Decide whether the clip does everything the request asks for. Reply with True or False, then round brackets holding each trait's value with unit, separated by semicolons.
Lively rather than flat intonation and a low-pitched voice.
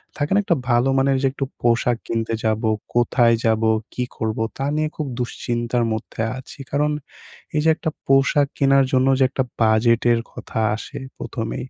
False (3.0 semitones; 120 Hz)